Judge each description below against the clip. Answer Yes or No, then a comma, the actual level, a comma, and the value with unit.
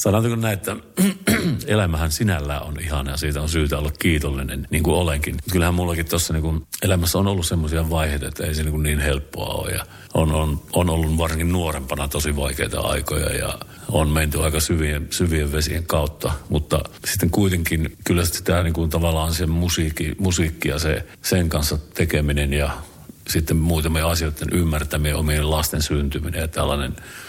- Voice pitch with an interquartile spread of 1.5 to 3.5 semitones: Yes, narrow, 2.5 semitones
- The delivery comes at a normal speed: No, fast, 170 wpm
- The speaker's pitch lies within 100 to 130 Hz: No, very low, 80 Hz